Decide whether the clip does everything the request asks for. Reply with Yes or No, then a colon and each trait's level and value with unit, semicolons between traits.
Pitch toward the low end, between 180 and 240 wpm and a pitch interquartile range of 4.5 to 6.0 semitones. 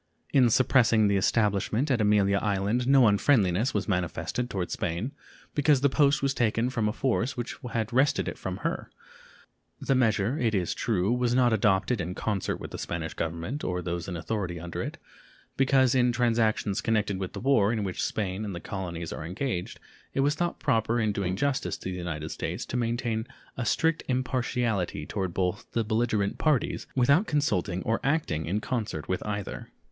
Yes: low, 110 Hz; average, 185 wpm; average, 4.8 semitones